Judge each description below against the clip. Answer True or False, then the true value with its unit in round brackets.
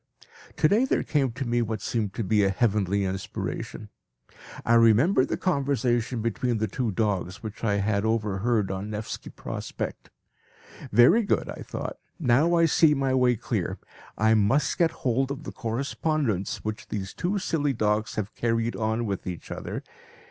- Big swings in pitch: False (4.4 semitones)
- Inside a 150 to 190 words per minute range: True (165 wpm)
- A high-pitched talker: False (115 Hz)